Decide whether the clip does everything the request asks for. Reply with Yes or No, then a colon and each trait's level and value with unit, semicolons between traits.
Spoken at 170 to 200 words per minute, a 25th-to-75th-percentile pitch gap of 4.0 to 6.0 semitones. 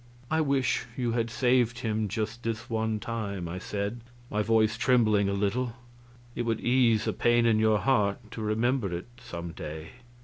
No: average, 175 wpm; narrow, 2.6 semitones